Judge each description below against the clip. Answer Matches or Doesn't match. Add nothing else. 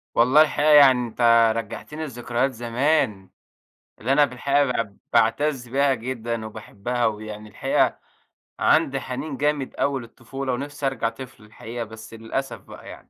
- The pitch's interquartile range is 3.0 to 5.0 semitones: Matches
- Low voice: Matches